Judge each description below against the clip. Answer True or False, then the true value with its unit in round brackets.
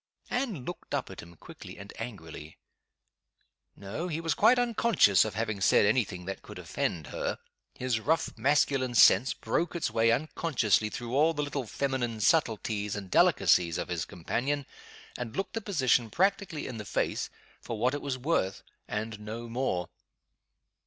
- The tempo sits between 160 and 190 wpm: True (165 wpm)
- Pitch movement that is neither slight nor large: False (5.9 semitones)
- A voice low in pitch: True (120 Hz)